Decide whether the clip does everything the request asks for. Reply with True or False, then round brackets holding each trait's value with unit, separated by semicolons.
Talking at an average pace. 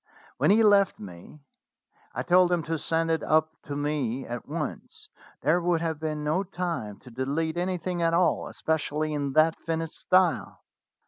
True (175 wpm)